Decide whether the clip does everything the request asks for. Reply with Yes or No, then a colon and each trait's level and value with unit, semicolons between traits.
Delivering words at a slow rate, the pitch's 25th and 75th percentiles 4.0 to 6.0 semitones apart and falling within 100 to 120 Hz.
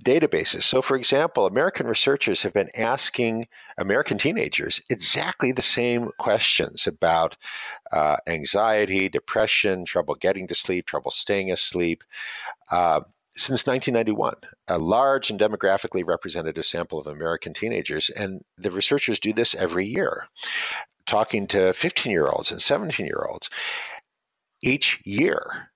Yes: slow, 130 wpm; average, 4.5 semitones; low, 105 Hz